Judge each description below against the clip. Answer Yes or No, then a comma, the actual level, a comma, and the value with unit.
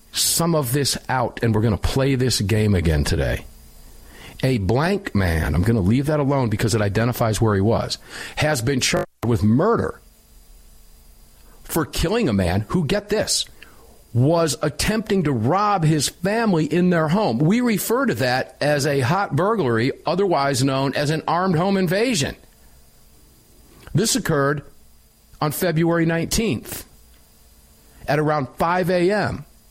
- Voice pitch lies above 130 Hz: Yes, medium, 140 Hz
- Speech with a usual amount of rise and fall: No, wide, 7.2 semitones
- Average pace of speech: Yes, average, 145 wpm